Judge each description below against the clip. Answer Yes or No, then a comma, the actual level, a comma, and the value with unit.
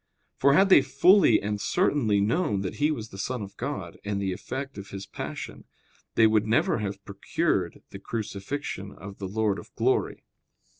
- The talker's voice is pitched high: No, low, 105 Hz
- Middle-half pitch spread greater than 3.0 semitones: Yes, wide, 5.6 semitones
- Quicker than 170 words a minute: Yes, average, 180 wpm